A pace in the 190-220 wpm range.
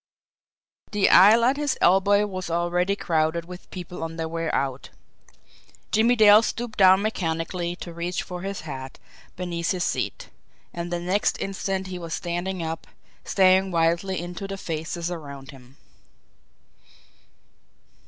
No: average, 140 wpm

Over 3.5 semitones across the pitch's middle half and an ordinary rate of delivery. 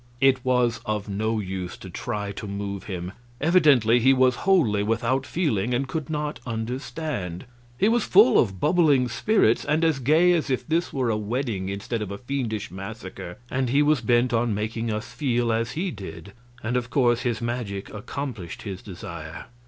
Yes: average, 4.7 semitones; average, 180 wpm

